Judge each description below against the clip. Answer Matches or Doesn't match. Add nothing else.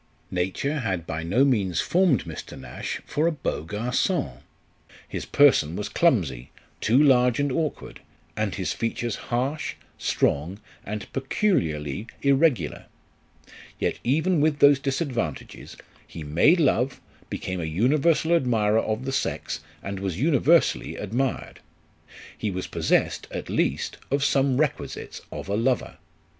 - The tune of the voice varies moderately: Doesn't match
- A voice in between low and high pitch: Doesn't match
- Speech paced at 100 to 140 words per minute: Matches